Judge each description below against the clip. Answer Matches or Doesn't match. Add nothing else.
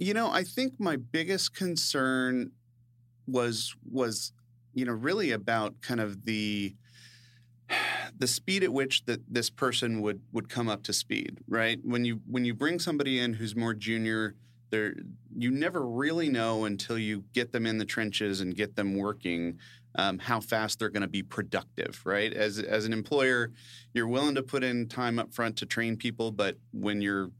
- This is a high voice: Doesn't match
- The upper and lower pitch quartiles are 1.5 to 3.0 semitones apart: Matches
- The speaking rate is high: Doesn't match